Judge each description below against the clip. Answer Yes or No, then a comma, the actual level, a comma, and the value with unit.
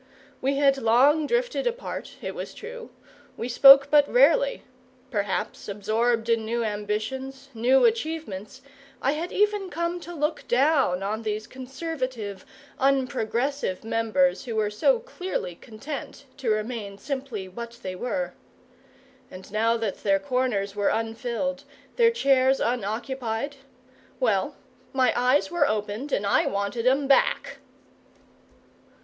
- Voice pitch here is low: No, very high, 255 Hz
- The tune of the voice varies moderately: Yes, average, 4.8 semitones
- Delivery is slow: Yes, slow, 130 wpm